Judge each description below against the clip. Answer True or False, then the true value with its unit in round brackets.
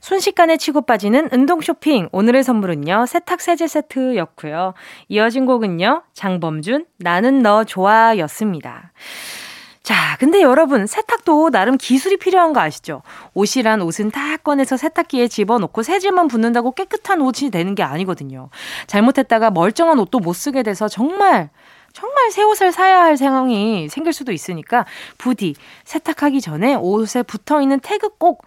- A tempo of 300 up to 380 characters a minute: True (335 characters per minute)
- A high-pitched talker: True (260 Hz)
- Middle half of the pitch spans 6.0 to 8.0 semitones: True (7.4 semitones)